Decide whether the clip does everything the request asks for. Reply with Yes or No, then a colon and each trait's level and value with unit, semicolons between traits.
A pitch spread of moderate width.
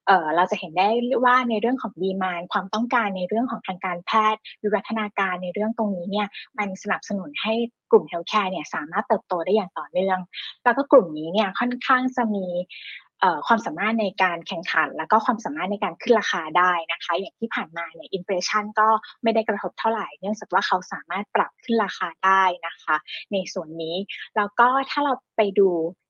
Yes: average, 3.7 semitones